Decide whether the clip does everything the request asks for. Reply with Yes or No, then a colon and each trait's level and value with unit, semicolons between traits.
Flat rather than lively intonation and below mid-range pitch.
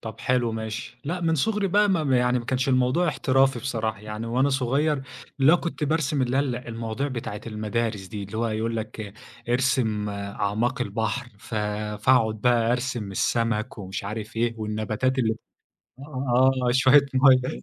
No: average, 3.3 semitones; low, 120 Hz